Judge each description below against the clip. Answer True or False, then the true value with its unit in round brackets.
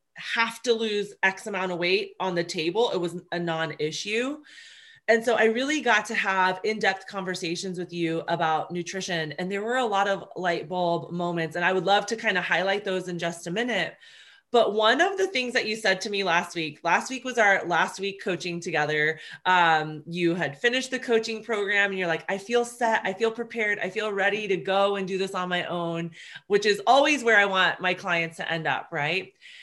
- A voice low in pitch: False (195 Hz)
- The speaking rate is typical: False (225 wpm)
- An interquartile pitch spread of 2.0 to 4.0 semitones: False (4.5 semitones)